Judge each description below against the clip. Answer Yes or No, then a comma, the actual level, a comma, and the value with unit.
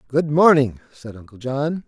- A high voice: No, medium, 140 Hz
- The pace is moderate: Yes, average, 160 wpm